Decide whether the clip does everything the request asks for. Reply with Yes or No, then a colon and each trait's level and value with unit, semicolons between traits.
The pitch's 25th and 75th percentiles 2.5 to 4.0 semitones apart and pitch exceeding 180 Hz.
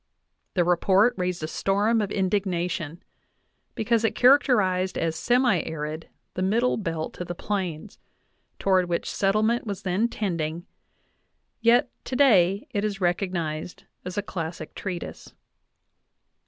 Yes: average, 3.5 semitones; high, 190 Hz